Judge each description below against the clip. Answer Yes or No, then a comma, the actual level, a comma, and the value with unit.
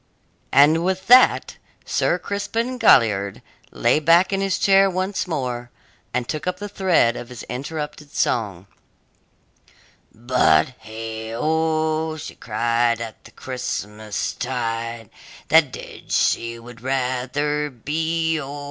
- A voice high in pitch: No, low, 135 Hz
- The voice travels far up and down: Yes, wide, 5.7 semitones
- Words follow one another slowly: Yes, slow, 120 wpm